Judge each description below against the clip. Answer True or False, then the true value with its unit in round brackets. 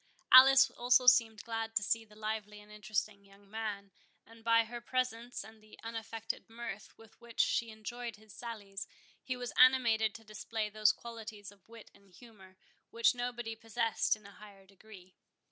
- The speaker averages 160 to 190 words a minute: True (170 wpm)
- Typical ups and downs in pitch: False (1.9 semitones)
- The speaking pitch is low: False (220 Hz)